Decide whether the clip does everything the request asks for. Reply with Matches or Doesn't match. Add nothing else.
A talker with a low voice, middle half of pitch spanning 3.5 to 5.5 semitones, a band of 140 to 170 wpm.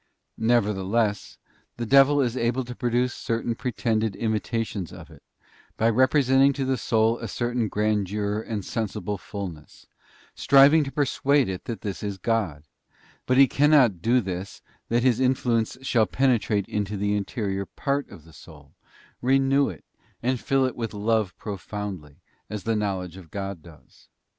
Matches